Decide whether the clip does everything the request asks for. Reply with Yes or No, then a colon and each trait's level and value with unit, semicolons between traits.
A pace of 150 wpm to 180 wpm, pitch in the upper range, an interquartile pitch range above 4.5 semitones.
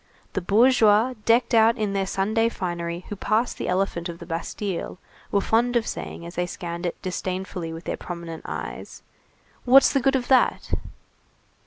Yes: average, 170 wpm; high, 195 Hz; average, 5.0 semitones